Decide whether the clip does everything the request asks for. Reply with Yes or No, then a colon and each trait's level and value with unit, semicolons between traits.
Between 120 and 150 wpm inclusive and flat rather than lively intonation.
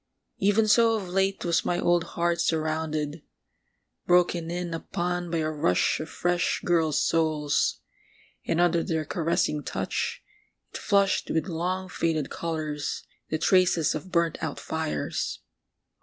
Yes: slow, 135 wpm; narrow, 2.1 semitones